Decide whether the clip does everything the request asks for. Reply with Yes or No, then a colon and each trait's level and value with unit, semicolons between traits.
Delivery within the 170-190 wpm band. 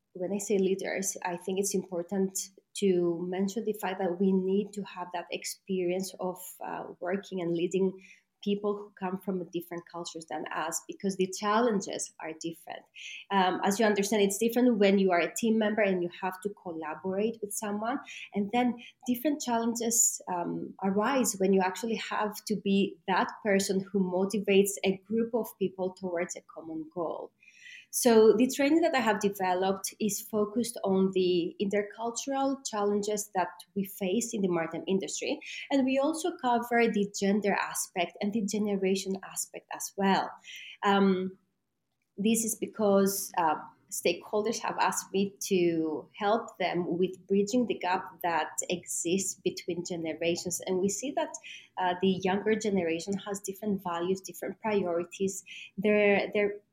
No: average, 155 wpm